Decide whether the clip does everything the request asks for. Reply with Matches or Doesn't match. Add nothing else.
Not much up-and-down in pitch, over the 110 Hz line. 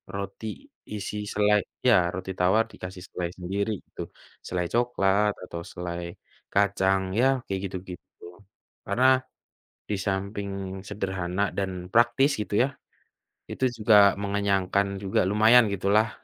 Doesn't match